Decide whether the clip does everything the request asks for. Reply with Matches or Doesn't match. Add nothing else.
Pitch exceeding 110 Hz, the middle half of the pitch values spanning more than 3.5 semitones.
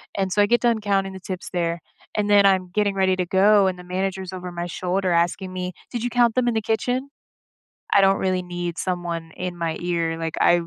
Doesn't match